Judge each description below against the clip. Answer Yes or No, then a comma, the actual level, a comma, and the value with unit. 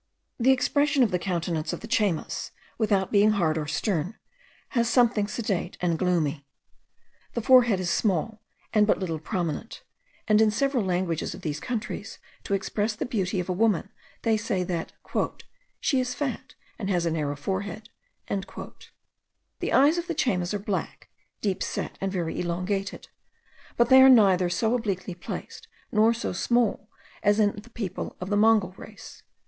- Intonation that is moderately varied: Yes, average, 4.0 semitones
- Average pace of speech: Yes, average, 165 wpm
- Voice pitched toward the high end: Yes, high, 200 Hz